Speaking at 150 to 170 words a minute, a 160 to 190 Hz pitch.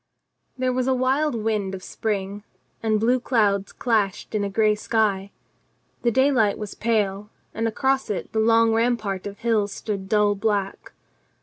No: average, 160 wpm; high, 215 Hz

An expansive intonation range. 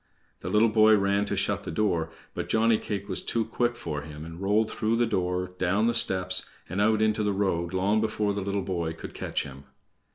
No: average, 3.2 semitones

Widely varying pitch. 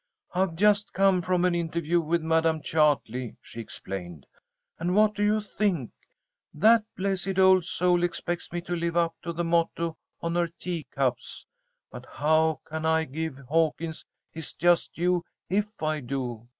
No: narrow, 2.5 semitones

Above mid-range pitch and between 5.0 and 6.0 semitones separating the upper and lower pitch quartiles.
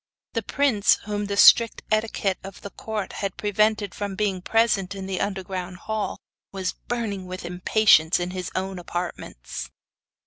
No: high, 195 Hz; narrow, 2.6 semitones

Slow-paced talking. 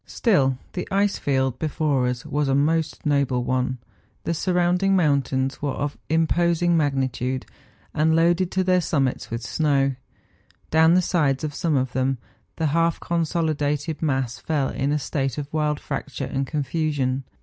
No: average, 165 wpm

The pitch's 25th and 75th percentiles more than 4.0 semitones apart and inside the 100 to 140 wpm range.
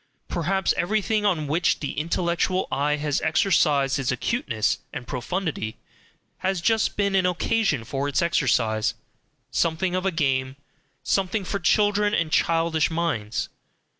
Yes: wide, 5.4 semitones; slow, 135 wpm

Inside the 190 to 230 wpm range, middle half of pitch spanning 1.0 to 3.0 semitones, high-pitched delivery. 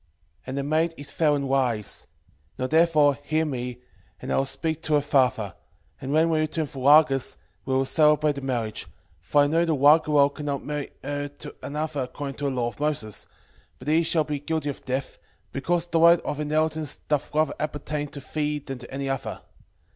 No: average, 200 wpm; narrow, 2.4 semitones; medium, 145 Hz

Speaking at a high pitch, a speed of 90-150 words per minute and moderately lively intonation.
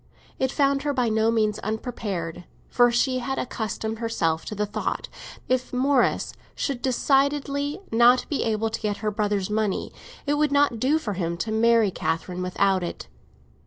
No: high, 225 Hz; average, 170 wpm; average, 4.1 semitones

